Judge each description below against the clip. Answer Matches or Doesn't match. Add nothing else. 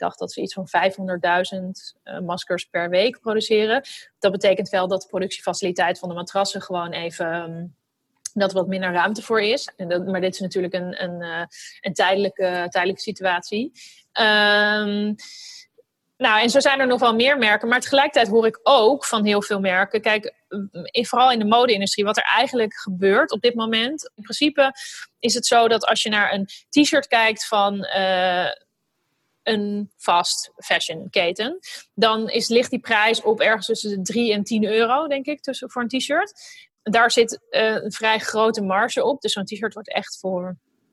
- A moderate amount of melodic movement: Matches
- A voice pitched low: Doesn't match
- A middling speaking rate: Matches